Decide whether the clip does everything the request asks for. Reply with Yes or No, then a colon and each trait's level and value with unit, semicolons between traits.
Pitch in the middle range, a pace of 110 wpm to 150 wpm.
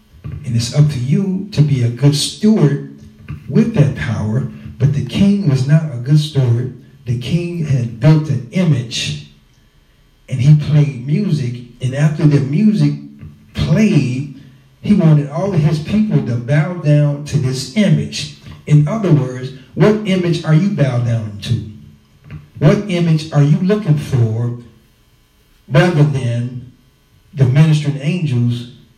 Yes: medium, 145 Hz; average, 145 wpm